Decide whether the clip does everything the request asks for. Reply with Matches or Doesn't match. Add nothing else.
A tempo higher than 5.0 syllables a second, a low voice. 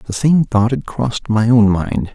Doesn't match